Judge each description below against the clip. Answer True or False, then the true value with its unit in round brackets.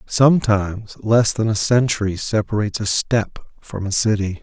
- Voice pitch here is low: True (105 Hz)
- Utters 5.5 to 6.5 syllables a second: False (5.1 syllables/s)